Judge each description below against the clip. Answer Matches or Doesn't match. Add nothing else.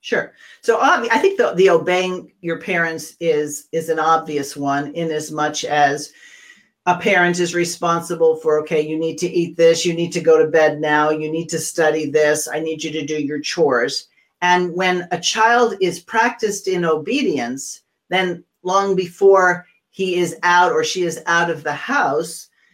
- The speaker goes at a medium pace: Matches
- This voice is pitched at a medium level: Matches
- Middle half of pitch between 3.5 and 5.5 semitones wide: Doesn't match